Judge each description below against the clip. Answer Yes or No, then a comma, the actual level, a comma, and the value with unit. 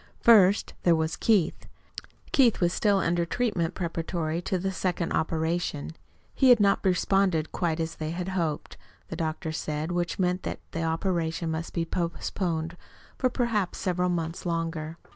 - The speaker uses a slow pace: No, average, 155 wpm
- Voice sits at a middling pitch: Yes, medium, 170 Hz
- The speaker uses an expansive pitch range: No, narrow, 2.6 semitones